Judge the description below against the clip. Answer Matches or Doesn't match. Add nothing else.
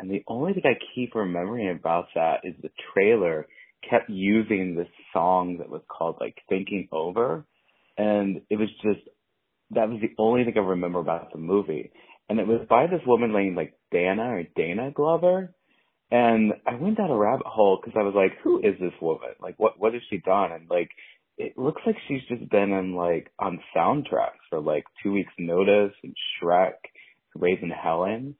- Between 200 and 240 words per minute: Doesn't match